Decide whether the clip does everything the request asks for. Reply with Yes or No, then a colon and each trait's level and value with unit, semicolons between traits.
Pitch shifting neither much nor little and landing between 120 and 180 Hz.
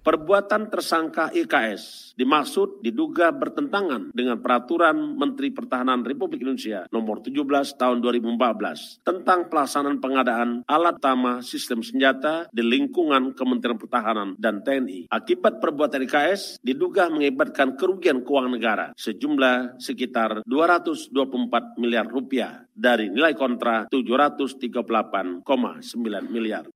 No: wide, 6.3 semitones; low, 135 Hz